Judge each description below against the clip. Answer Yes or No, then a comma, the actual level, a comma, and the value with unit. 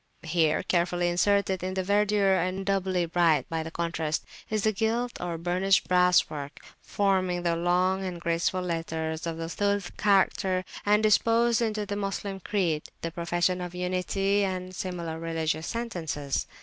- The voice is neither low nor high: Yes, medium, 180 Hz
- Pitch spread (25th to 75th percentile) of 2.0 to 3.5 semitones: Yes, average, 2.8 semitones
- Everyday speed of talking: Yes, average, 150 wpm